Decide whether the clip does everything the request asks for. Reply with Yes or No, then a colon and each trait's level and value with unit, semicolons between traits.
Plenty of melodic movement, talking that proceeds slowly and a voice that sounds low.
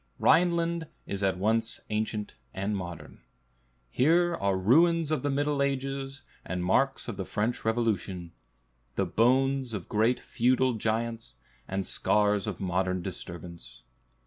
Yes: wide, 6.0 semitones; slow, 130 wpm; low, 110 Hz